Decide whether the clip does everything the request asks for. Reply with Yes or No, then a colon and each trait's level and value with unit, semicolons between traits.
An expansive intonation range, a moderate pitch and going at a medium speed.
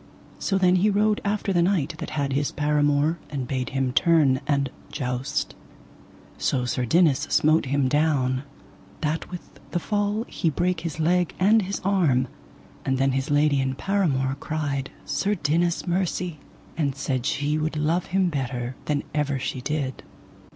No: average, 4.6 semitones; medium, 150 Hz; average, 160 wpm